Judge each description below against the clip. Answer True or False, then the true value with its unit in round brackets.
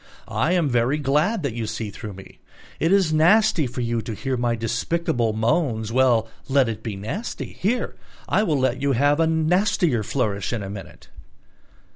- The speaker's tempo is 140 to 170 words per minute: False (180 wpm)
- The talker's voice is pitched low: True (130 Hz)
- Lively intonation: True (6.1 semitones)